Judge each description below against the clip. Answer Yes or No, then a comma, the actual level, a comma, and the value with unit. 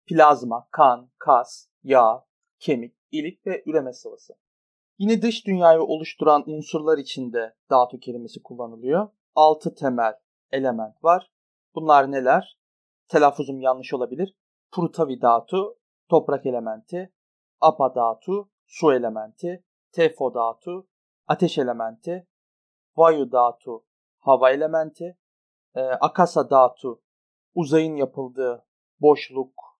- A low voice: No, medium, 150 Hz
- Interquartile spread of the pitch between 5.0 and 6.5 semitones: Yes, wide, 5.6 semitones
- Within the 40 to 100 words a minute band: Yes, slow, 95 wpm